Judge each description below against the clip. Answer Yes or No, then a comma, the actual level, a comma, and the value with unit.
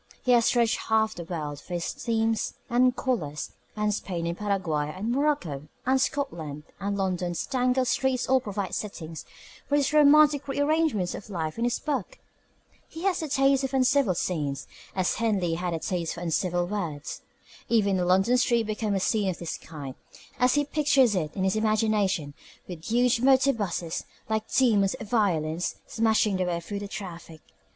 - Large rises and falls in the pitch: Yes, wide, 6.3 semitones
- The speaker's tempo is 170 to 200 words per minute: Yes, average, 175 wpm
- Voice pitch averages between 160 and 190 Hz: No, high, 210 Hz